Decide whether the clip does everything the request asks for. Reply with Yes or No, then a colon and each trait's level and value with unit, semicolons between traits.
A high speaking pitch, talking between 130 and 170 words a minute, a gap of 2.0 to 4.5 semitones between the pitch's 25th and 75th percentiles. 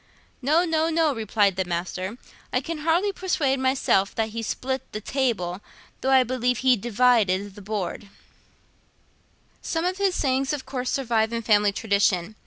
No: high, 245 Hz; average, 160 wpm; average, 5.0 semitones